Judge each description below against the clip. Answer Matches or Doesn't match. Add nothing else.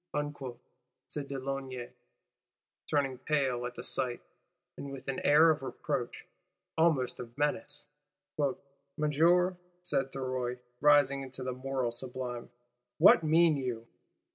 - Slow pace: Matches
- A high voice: Doesn't match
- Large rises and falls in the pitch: Doesn't match